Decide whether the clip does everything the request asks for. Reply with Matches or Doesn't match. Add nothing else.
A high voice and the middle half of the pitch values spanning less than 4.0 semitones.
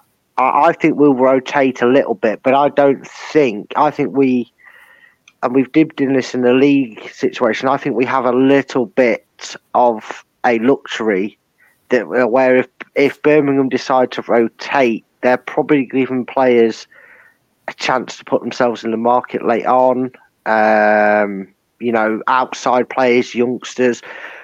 Doesn't match